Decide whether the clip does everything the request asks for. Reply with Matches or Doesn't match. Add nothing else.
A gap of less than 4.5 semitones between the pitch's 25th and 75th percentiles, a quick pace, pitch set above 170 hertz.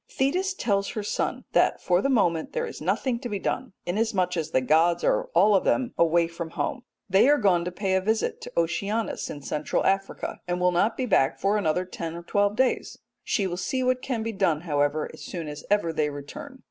Doesn't match